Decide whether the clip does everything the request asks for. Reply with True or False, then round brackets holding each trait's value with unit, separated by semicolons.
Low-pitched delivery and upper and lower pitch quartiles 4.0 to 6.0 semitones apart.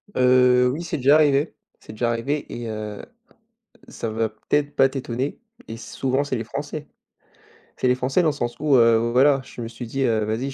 False (125 Hz; 3.5 semitones)